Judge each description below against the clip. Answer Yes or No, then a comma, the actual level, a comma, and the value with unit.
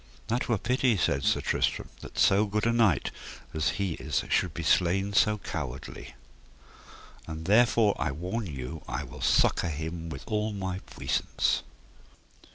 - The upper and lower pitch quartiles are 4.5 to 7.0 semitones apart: Yes, average, 4.8 semitones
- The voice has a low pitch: Yes, very low, 95 Hz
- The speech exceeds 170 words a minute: No, average, 155 wpm